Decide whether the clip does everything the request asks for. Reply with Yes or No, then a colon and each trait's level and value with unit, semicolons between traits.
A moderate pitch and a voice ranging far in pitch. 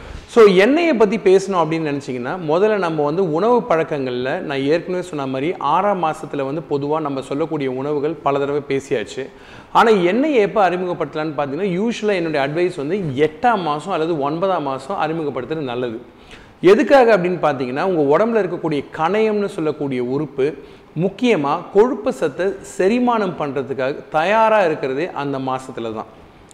Yes: medium, 160 Hz; wide, 6.1 semitones